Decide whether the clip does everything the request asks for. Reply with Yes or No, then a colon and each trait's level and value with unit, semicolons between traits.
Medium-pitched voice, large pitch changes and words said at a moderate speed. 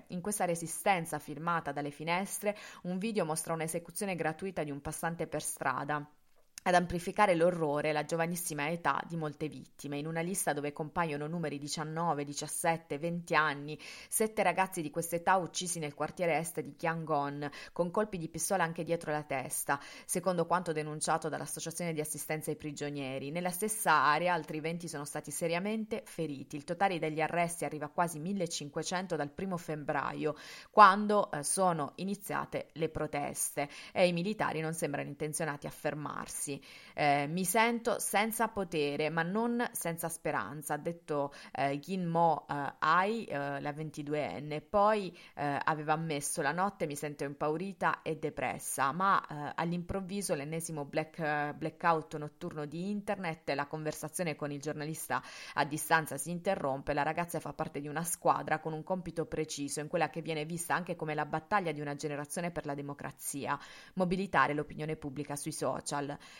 No: medium, 160 Hz; average, 2.9 semitones; average, 160 wpm